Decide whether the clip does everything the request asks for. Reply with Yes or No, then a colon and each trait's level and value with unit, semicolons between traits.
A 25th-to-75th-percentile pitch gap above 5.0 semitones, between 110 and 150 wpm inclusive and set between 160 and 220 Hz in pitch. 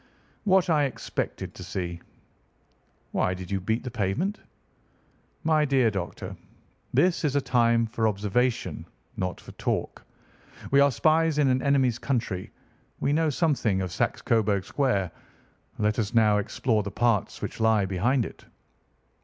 No: wide, 5.5 semitones; average, 145 wpm; low, 115 Hz